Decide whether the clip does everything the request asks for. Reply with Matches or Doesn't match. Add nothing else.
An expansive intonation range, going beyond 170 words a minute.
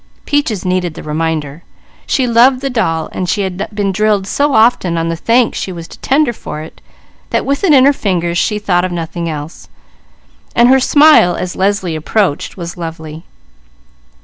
Matches